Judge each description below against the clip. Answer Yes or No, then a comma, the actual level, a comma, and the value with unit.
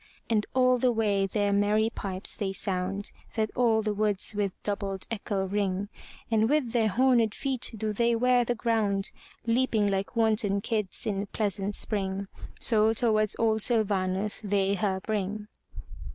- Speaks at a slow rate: No, average, 150 wpm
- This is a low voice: No, high, 210 Hz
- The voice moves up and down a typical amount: No, narrow, 2.2 semitones